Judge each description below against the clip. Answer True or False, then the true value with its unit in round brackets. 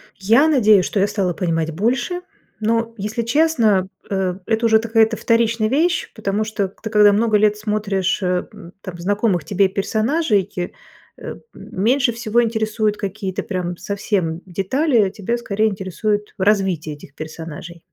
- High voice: True (210 Hz)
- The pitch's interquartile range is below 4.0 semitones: True (3.2 semitones)